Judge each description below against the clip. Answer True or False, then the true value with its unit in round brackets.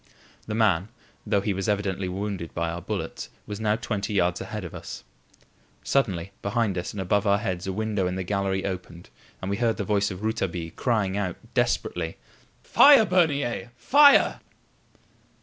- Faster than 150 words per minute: True (165 wpm)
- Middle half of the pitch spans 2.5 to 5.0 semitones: True (3.0 semitones)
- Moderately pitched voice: False (100 Hz)